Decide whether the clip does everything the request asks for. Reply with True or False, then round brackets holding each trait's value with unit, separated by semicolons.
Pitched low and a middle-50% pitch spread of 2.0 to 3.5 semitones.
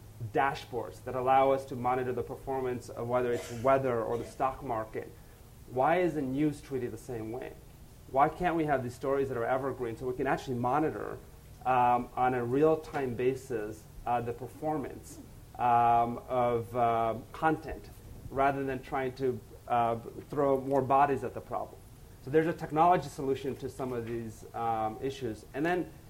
True (125 Hz; 2.5 semitones)